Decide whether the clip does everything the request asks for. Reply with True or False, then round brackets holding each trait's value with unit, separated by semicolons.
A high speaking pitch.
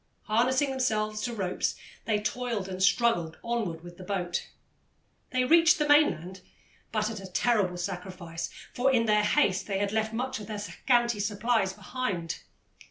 True (215 Hz)